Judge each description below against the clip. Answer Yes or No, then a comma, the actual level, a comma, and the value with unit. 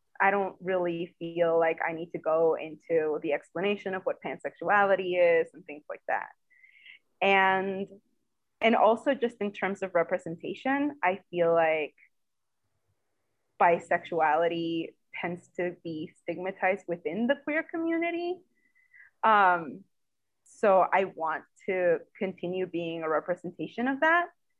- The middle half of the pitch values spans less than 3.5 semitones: No, average, 3.8 semitones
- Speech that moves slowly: Yes, slow, 125 wpm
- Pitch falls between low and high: Yes, medium, 180 Hz